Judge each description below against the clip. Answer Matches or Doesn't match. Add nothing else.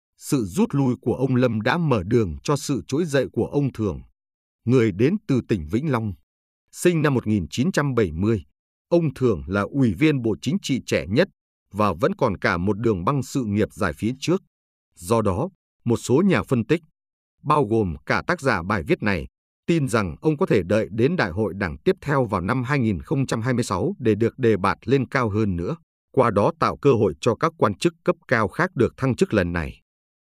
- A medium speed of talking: Matches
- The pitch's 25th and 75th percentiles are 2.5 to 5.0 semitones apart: Doesn't match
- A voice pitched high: Doesn't match